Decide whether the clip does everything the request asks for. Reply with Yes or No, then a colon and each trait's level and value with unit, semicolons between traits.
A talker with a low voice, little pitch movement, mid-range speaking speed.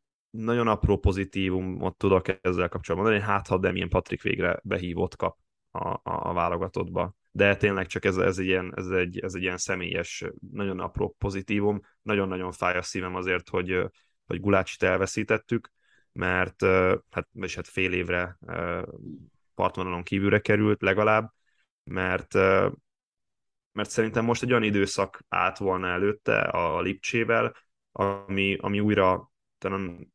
Yes: very low, 95 Hz; narrow, 2.0 semitones; average, 135 wpm